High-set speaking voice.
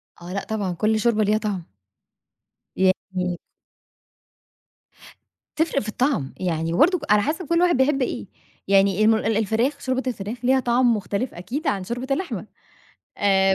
Yes: high, 220 Hz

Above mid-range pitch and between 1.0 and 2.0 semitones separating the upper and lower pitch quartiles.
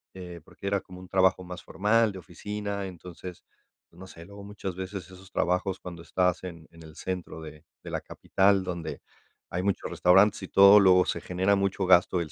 No: very low, 95 Hz; narrow, 1.7 semitones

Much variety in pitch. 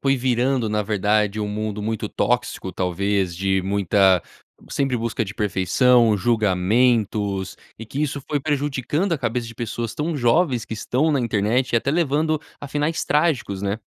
No: average, 5.0 semitones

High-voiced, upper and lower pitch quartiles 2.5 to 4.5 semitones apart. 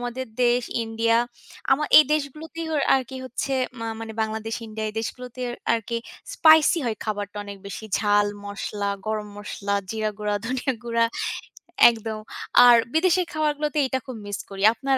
Yes: high, 230 Hz; average, 3.8 semitones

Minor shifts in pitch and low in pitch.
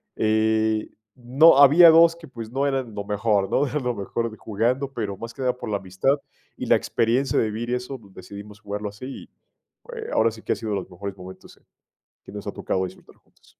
No: average, 4.4 semitones; low, 115 Hz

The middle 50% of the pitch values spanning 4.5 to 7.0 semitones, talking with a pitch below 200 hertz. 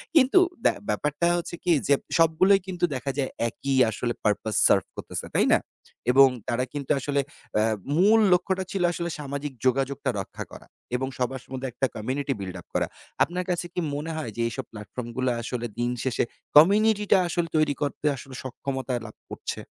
Yes: average, 5.3 semitones; medium, 140 Hz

